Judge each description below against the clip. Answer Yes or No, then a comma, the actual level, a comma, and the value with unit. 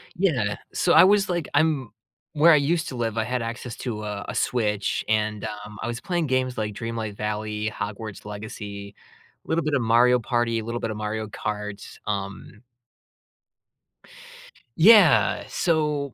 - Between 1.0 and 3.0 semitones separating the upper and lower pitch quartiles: No, average, 5.0 semitones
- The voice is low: Yes, low, 115 Hz